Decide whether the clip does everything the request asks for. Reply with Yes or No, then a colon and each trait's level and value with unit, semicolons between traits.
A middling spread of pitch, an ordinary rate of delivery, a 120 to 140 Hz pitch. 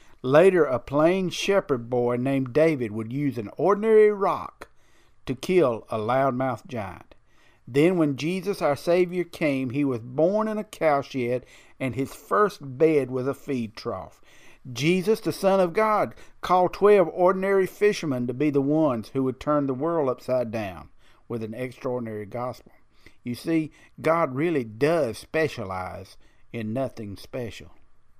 No: wide, 5.8 semitones; average, 150 wpm; low, 135 Hz